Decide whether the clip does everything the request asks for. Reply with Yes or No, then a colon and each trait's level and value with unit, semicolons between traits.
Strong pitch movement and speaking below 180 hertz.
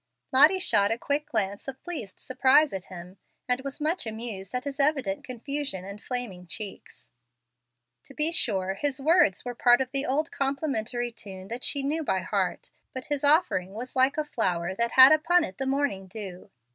No: wide, 6.2 semitones; very high, 255 Hz